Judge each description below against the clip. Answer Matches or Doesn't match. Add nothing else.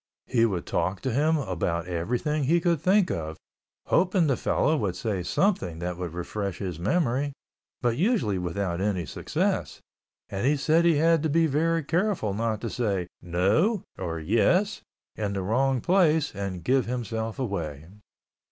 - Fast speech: Doesn't match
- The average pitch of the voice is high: Doesn't match